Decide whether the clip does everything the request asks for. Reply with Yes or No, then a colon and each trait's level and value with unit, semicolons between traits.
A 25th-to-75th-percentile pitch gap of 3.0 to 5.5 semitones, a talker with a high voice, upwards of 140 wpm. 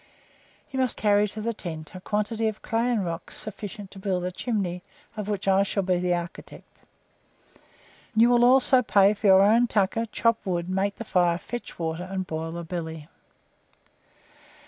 Yes: average, 3.7 semitones; high, 200 Hz; average, 175 wpm